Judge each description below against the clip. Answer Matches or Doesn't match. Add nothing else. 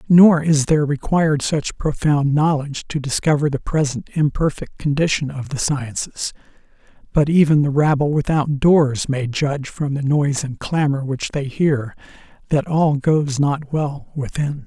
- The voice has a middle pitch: Matches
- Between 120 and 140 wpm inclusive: Doesn't match